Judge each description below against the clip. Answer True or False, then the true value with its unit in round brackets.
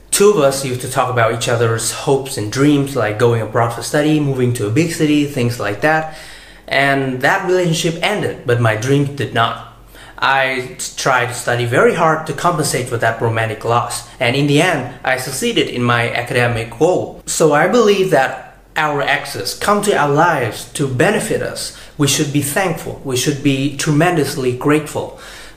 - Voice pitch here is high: False (135 Hz)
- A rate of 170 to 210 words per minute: True (185 wpm)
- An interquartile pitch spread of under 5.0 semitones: True (4.3 semitones)